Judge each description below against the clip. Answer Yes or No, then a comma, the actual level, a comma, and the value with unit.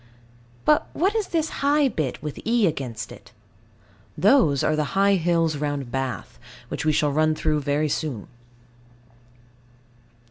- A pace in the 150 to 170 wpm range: No, slow, 135 wpm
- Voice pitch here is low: No, medium, 155 Hz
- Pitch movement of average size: No, wide, 5.8 semitones